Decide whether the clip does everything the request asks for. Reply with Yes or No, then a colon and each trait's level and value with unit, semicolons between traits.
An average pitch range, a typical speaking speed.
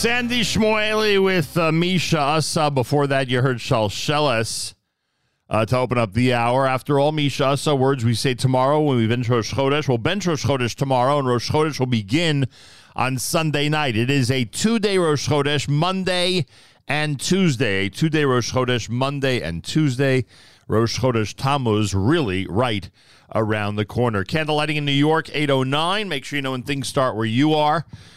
Yes: average, 4.1 semitones; average, 180 wpm